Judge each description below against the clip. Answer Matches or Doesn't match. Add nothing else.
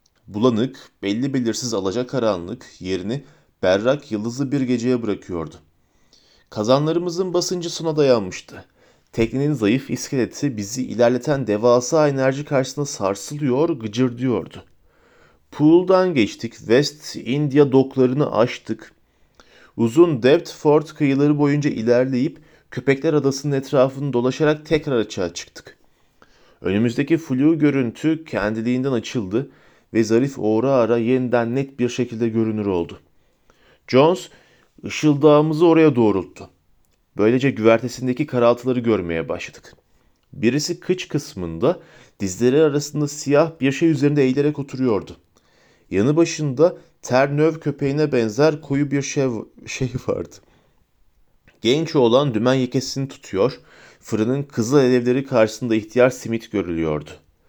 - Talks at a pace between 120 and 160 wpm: Doesn't match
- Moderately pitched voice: Doesn't match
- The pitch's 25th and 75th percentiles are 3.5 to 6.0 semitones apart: Matches